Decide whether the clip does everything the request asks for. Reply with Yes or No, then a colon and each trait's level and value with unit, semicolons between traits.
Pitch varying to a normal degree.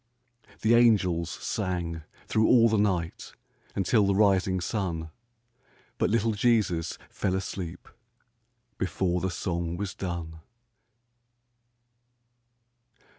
Yes: average, 3.4 semitones